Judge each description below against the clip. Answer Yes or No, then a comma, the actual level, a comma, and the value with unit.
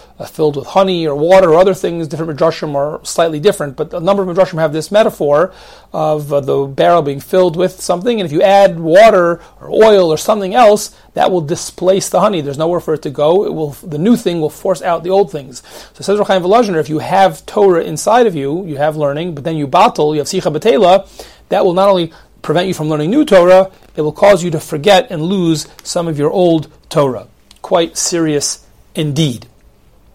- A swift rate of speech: Yes, fast, 215 wpm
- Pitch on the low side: No, medium, 170 Hz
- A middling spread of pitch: Yes, average, 3.8 semitones